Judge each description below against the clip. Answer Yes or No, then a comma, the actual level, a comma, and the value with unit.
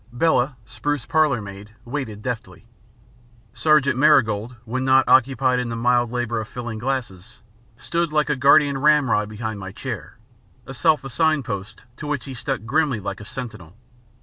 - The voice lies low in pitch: Yes, low, 125 Hz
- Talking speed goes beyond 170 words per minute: No, average, 160 wpm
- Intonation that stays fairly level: No, average, 3.9 semitones